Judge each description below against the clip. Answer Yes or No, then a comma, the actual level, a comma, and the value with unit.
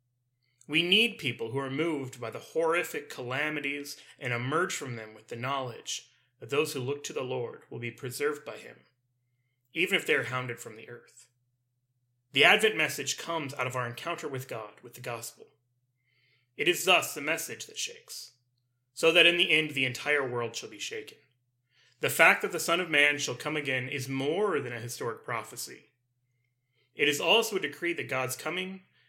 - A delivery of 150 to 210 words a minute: Yes, average, 190 wpm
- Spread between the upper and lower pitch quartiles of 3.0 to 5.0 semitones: Yes, average, 3.7 semitones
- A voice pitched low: Yes, low, 130 Hz